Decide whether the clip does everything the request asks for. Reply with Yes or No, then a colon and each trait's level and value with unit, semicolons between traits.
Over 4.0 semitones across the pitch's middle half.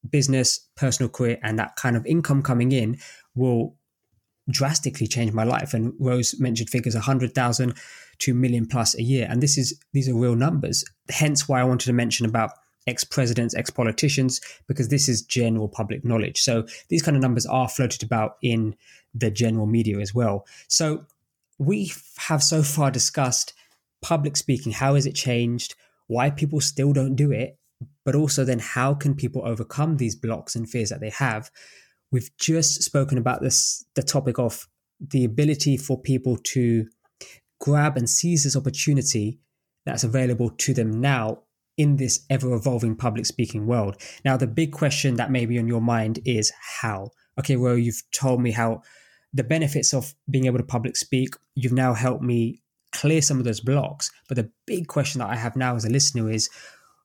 No: average, 2.8 semitones